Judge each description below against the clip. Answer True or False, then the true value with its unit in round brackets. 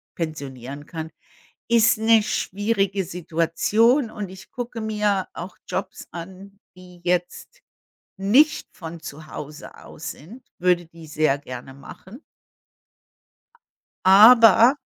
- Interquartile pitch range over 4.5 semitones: True (5.2 semitones)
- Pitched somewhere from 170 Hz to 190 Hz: True (185 Hz)